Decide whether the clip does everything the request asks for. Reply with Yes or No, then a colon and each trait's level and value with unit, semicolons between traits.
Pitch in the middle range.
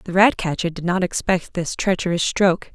Yes: medium, 180 Hz